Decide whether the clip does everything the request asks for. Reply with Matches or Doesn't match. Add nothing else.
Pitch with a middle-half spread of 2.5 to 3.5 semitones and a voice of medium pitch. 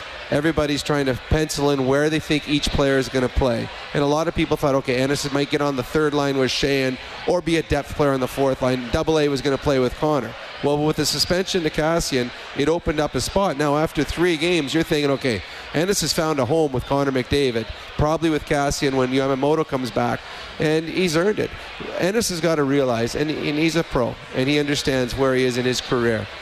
Matches